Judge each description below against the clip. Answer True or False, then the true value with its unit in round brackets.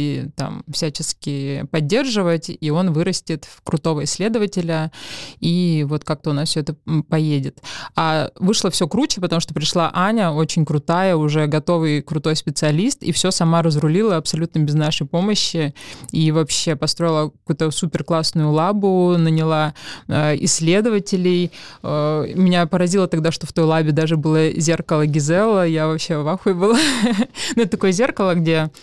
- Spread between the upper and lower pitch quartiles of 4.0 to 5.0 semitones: False (2.7 semitones)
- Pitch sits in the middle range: True (165 Hz)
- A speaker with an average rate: True (145 wpm)